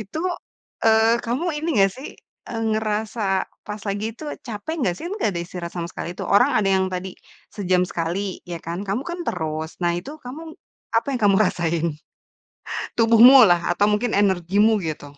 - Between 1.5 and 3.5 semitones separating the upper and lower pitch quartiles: No, average, 4.4 semitones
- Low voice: No, high, 205 Hz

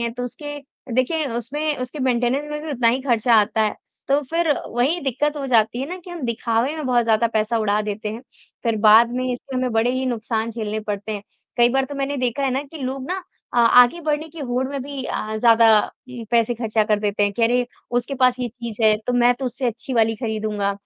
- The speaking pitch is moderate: No, high, 245 Hz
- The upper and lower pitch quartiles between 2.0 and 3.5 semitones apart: Yes, average, 3.2 semitones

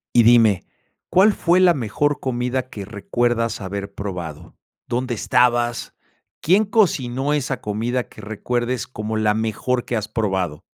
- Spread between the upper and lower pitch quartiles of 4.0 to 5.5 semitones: No, average, 3.4 semitones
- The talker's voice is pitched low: Yes, low, 120 Hz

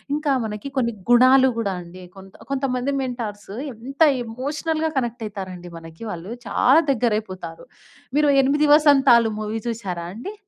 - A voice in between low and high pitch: No, high, 235 Hz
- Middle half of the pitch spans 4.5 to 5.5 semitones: Yes, average, 5.1 semitones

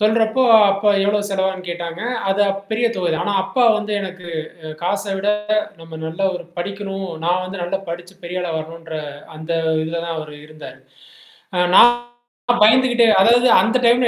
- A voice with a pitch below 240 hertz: Yes, high, 190 Hz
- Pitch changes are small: No, average, 3.7 semitones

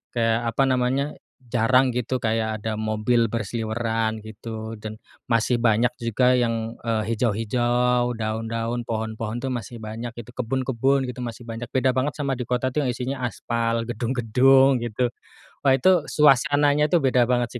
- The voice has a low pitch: Yes, low, 120 Hz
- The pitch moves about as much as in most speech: No, narrow, 2.2 semitones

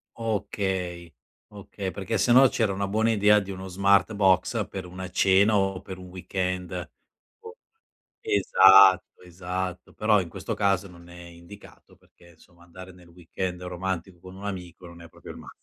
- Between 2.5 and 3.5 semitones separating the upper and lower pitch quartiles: No, narrow, 1.9 semitones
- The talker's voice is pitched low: Yes, very low, 95 Hz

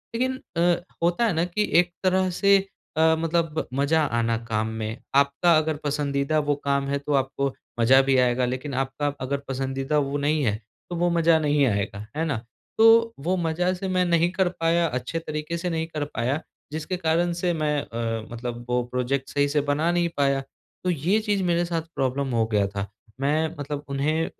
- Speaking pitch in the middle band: Yes, medium, 150 Hz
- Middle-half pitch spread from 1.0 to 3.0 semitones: No, average, 4.2 semitones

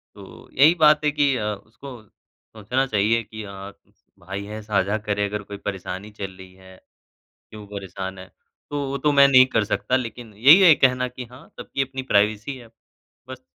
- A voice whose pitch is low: Yes, low, 110 Hz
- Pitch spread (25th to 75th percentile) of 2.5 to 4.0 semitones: No, average, 4.8 semitones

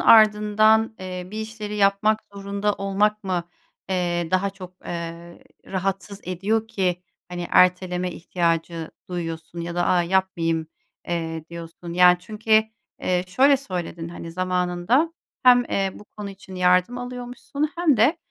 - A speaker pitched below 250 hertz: Yes, medium, 185 Hz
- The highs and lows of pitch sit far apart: No, average, 3.4 semitones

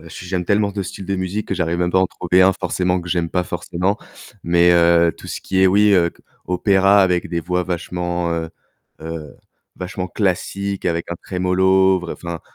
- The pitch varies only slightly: Yes, narrow, 1.7 semitones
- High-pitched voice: No, very low, 90 Hz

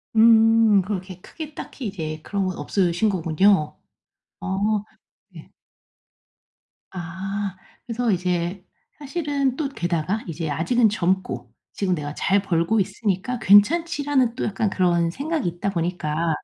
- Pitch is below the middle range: No, high, 195 Hz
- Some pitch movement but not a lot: Yes, average, 4.7 semitones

